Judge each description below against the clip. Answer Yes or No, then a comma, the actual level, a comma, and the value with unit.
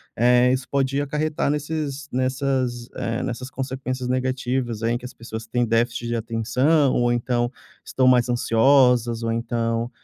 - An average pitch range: No, narrow, 2.1 semitones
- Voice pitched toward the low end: Yes, low, 125 Hz